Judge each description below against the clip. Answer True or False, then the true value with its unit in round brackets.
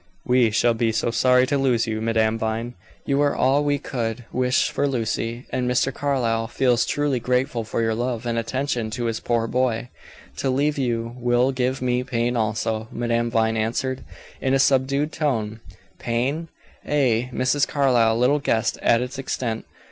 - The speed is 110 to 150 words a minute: False (170 wpm)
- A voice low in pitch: True (125 Hz)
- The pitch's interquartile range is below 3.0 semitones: True (2.5 semitones)